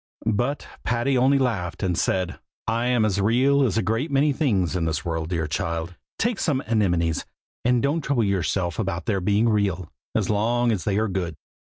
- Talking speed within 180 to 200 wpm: Yes, average, 190 wpm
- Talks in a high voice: No, low, 105 Hz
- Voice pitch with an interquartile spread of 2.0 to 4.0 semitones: No, wide, 5.4 semitones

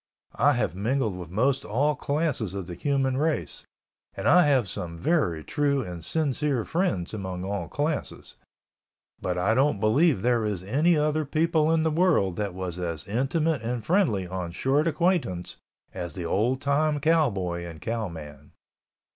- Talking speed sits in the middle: Yes, average, 155 wpm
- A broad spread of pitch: Yes, wide, 8.5 semitones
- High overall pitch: No, low, 120 Hz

